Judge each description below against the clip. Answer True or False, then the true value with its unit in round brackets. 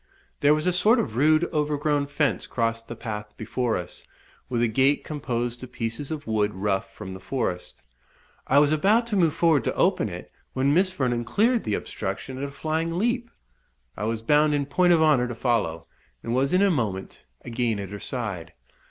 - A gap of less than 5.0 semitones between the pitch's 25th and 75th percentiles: False (5.4 semitones)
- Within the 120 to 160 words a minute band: False (195 wpm)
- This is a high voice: False (130 Hz)